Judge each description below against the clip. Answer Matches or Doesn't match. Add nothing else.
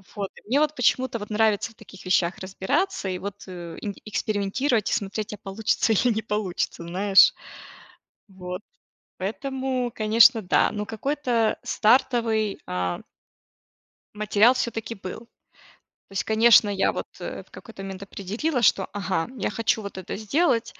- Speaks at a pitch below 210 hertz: Doesn't match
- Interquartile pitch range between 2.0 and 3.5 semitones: Matches